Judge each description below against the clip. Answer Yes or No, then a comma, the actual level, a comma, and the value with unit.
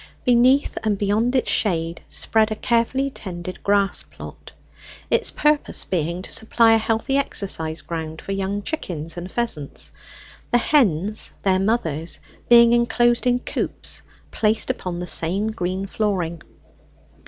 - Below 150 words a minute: Yes, slow, 135 wpm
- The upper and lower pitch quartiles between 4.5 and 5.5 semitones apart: Yes, average, 5.2 semitones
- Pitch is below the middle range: No, high, 205 Hz